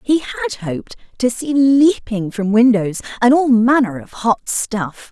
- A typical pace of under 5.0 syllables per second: Yes, 4.0 syllables/s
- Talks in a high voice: Yes, high, 240 Hz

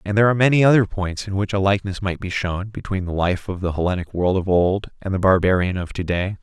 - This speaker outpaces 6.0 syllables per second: Yes, 6.3 syllables/s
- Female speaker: No, male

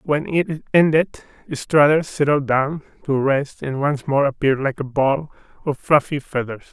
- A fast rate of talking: No, average, 160 wpm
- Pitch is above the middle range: No, medium, 140 Hz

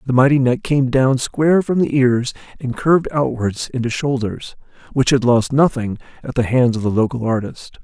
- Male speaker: Yes, male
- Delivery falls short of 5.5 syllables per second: Yes, 5.1 syllables/s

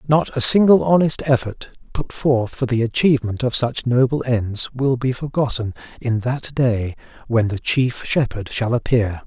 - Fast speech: No, average, 170 wpm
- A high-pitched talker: No, low, 125 Hz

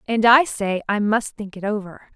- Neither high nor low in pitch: No, high, 210 Hz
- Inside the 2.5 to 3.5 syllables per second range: No, 4.7 syllables/s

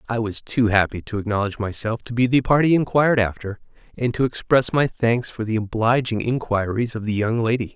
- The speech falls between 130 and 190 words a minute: No, average, 200 wpm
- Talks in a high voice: No, low, 115 Hz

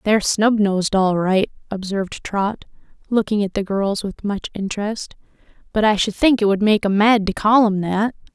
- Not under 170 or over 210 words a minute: Yes, average, 185 wpm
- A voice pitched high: Yes, high, 205 Hz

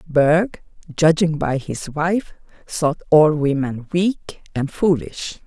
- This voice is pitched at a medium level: Yes, medium, 155 Hz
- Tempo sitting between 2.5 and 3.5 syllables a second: Yes, 3.2 syllables/s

